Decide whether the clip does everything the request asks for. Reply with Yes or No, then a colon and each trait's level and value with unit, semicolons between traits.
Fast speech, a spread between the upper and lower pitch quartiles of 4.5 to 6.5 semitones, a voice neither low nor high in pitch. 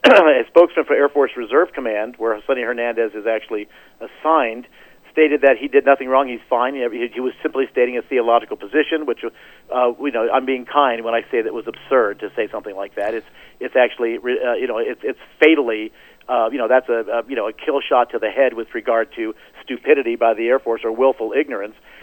No: fast, 220 wpm; average, 5.0 semitones; low, 130 Hz